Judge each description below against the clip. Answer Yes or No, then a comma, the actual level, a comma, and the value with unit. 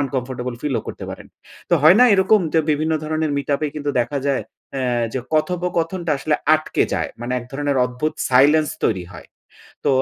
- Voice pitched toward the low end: No, medium, 145 Hz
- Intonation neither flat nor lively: Yes, average, 3.8 semitones